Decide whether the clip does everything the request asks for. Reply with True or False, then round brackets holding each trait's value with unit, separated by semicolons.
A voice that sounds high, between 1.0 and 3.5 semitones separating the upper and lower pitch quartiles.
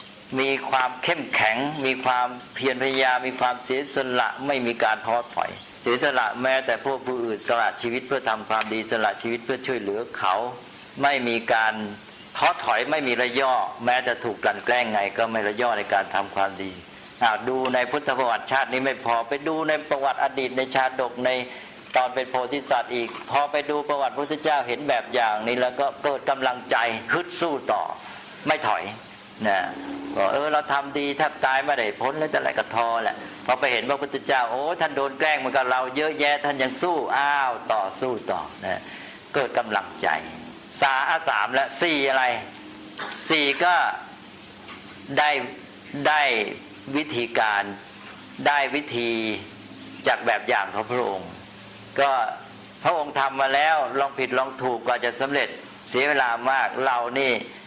False (130 Hz; 3.1 semitones)